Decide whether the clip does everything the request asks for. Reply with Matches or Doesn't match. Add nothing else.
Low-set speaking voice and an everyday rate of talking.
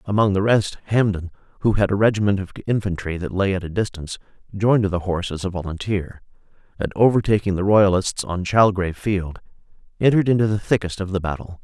Matches